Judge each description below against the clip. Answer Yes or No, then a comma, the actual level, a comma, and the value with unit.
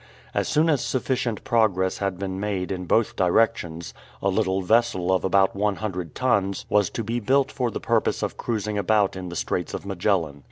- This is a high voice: No, low, 100 Hz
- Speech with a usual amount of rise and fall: Yes, average, 3.4 semitones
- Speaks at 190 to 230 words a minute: Yes, average, 195 wpm